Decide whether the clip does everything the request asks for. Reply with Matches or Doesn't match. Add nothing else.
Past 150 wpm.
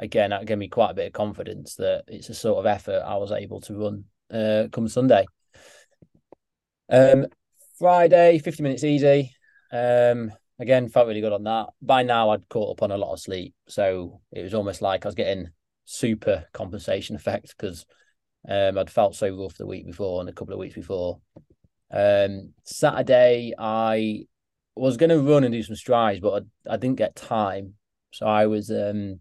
Matches